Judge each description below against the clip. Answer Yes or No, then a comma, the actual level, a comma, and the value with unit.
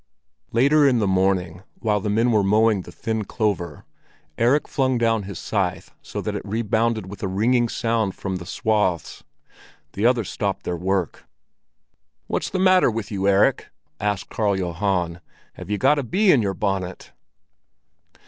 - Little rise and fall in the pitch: No, average, 3.5 semitones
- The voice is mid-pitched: No, low, 105 Hz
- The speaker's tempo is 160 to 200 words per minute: Yes, average, 165 wpm